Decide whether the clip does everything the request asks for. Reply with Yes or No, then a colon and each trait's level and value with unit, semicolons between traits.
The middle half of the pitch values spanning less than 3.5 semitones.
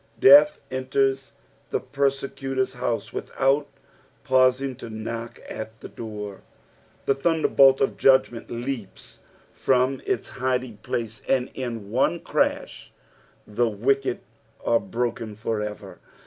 Yes: average, 2.9 semitones